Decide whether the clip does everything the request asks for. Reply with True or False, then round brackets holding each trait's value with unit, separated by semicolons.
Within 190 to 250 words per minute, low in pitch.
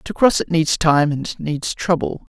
False (205 wpm; 160 Hz)